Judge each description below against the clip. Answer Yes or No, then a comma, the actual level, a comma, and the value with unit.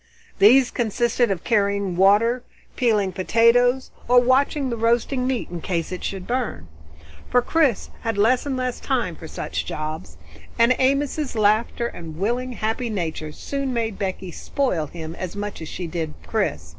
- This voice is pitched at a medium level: No, high, 220 Hz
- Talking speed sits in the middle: Yes, average, 160 wpm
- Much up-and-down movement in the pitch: Yes, wide, 5.7 semitones